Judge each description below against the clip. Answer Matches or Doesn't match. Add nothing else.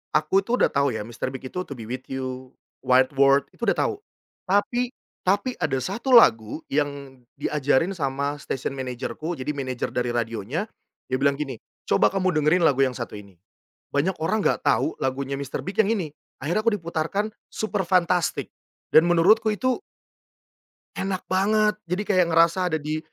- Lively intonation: Matches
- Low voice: Doesn't match